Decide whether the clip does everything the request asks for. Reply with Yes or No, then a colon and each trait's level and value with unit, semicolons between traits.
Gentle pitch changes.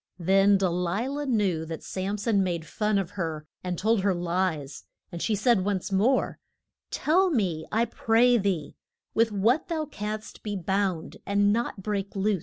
No: average, 3.6 semitones